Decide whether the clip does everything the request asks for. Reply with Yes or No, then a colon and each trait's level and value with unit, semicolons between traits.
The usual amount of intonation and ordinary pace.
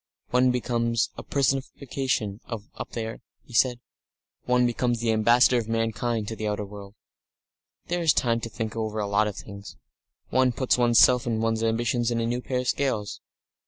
No: narrow, 2.2 semitones; average, 180 wpm